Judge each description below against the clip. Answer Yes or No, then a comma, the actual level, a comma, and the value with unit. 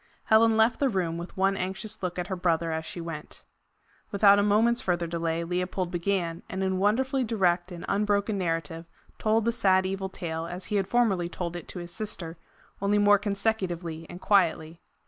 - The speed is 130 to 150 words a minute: No, average, 185 wpm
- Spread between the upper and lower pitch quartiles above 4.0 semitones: No, average, 3.2 semitones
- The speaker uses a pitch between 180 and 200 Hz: Yes, medium, 185 Hz